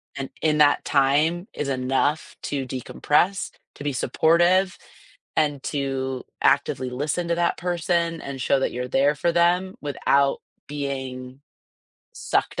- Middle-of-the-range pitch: Yes, medium, 145 Hz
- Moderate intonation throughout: Yes, average, 4.1 semitones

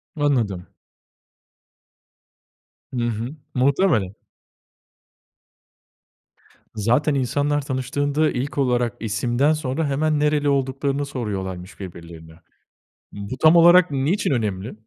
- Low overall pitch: Yes, low, 130 Hz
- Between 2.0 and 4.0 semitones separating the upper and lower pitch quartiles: No, average, 5.1 semitones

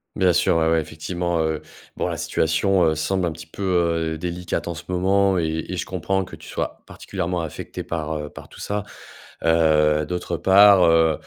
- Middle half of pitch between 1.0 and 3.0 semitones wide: Yes, narrow, 2.4 semitones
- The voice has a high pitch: No, very low, 85 Hz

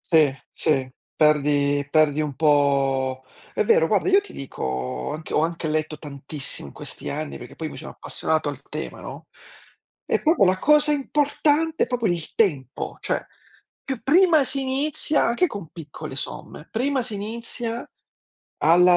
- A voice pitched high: No, medium, 160 Hz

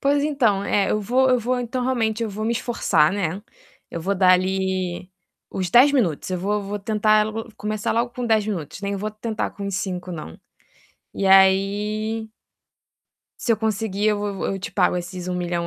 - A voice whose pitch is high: Yes, high, 205 Hz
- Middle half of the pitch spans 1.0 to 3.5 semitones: Yes, average, 2.9 semitones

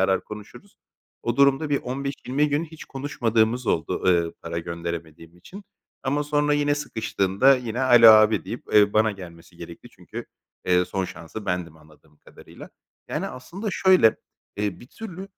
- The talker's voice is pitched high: No, low, 110 Hz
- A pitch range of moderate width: No, wide, 7.8 semitones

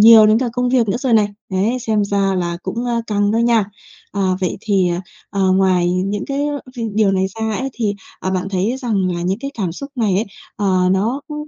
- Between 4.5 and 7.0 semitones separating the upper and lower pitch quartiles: No, average, 3.6 semitones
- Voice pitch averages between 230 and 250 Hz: No, high, 205 Hz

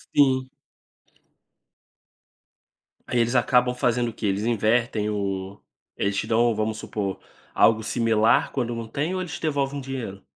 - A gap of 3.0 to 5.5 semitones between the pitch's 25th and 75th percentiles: Yes, average, 3.3 semitones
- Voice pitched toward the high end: No, low, 115 Hz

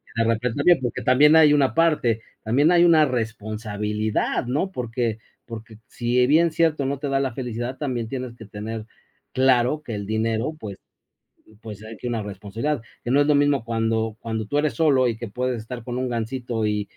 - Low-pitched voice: Yes, low, 120 Hz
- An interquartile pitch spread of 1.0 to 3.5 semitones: No, average, 3.9 semitones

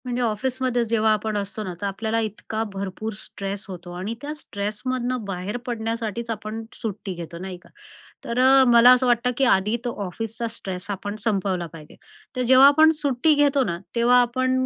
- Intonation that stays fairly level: No, average, 3.8 semitones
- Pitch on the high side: Yes, high, 225 Hz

